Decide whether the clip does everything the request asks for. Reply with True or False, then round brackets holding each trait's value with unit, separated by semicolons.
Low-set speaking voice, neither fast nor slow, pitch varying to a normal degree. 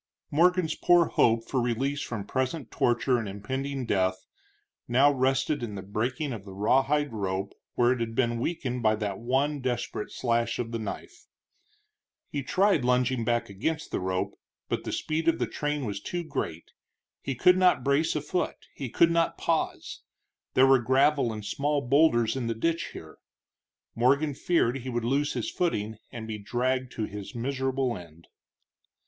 True (125 Hz; 170 wpm; 4.2 semitones)